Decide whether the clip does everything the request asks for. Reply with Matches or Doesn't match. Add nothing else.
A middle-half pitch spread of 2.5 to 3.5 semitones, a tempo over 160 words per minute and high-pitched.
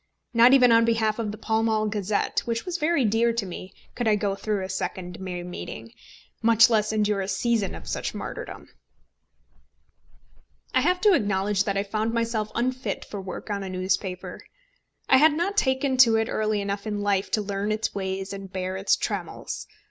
Matches